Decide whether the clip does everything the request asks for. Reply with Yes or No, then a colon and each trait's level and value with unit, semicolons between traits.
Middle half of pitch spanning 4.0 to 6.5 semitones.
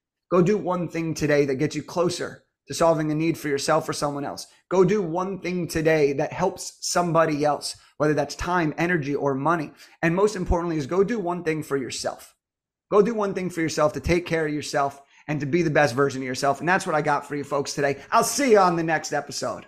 No: average, 3.5 semitones